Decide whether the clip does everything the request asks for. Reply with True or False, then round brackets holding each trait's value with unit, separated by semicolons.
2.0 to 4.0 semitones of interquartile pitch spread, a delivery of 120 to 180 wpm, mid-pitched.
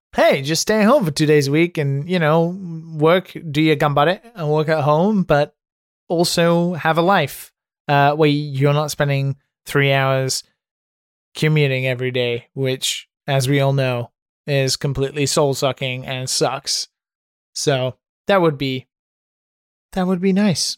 True (3.3 semitones; 155 wpm; 150 Hz)